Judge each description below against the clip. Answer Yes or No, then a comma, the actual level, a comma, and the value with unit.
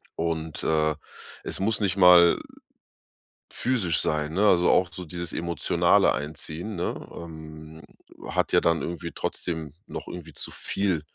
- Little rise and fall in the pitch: Yes, narrow, 2.3 semitones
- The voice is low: Yes, very low, 85 Hz